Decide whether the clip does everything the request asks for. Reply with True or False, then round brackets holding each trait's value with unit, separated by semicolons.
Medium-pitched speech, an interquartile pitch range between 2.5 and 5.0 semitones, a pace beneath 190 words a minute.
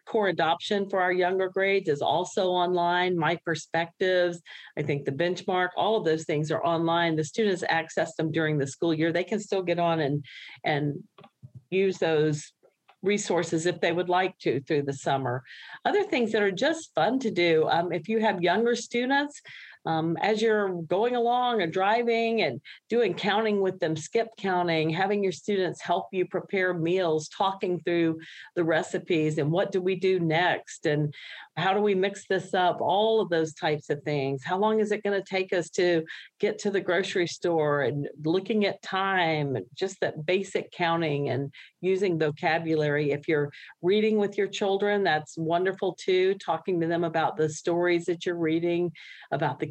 True (175 Hz; 3.4 semitones; 180 wpm)